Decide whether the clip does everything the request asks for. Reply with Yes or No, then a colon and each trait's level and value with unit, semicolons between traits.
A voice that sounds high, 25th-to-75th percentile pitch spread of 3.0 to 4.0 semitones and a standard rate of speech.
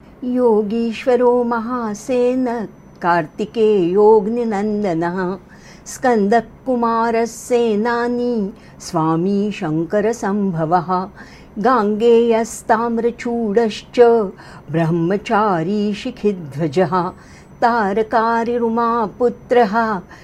No: high, 220 Hz; average, 3.3 semitones; slow, 35 wpm